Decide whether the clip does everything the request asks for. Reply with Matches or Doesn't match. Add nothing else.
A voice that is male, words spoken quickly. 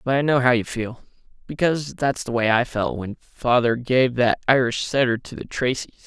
Matches